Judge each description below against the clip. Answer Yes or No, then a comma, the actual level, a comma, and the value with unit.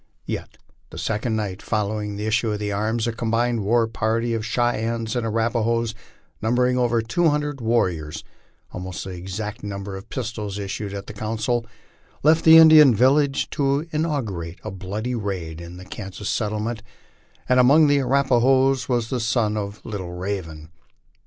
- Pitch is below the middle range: Yes, low, 110 Hz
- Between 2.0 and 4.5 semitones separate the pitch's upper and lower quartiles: Yes, average, 3.4 semitones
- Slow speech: No, average, 160 wpm